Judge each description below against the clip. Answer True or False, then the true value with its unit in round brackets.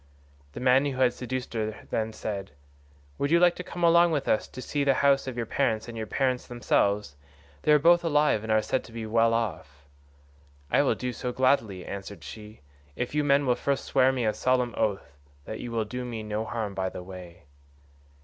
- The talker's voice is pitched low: True (120 Hz)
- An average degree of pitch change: True (3.9 semitones)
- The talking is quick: True (215 wpm)